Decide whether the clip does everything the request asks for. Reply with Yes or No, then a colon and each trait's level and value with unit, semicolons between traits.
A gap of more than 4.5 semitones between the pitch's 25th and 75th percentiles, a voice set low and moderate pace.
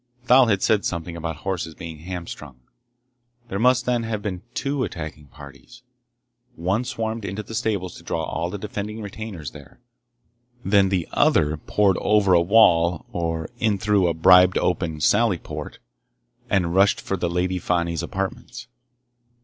No: average, 4.1 semitones; very low, 95 Hz; average, 150 wpm